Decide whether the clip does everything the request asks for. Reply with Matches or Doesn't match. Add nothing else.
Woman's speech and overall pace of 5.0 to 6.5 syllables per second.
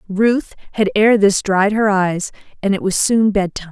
Doesn't match